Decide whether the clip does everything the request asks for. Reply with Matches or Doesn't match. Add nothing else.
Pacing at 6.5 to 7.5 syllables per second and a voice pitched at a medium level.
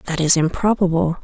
Doesn't match